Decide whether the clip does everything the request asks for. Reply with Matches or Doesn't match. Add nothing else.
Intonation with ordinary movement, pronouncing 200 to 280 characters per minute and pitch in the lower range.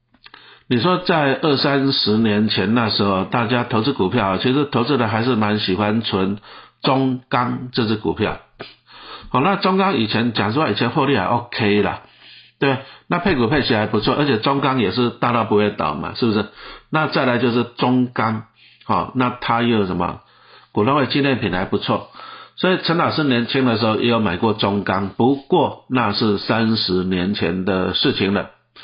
Matches